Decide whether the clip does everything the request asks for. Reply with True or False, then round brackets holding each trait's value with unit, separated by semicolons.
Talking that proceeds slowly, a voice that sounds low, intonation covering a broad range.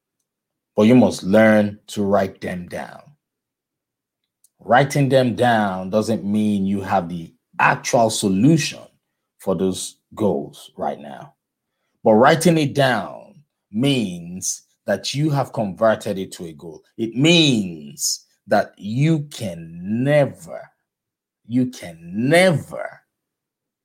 True (115 wpm; 115 Hz; 6.6 semitones)